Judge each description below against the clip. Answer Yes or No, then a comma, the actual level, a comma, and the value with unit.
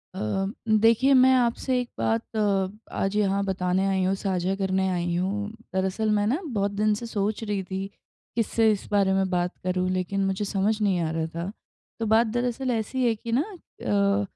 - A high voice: Yes, high, 200 Hz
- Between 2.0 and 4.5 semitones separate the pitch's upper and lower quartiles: Yes, average, 2.7 semitones